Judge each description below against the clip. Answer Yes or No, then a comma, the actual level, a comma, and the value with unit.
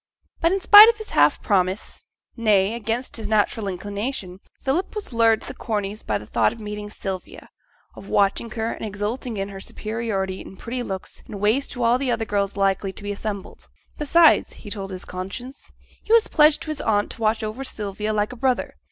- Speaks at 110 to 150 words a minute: No, fast, 205 wpm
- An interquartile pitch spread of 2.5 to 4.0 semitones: Yes, average, 3.7 semitones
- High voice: Yes, high, 215 Hz